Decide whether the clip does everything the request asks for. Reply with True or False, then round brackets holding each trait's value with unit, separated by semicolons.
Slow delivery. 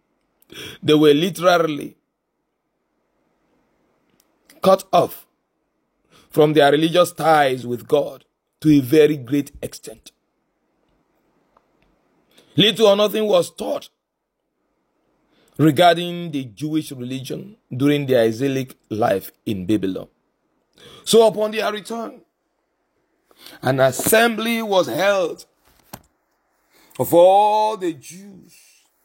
True (90 wpm)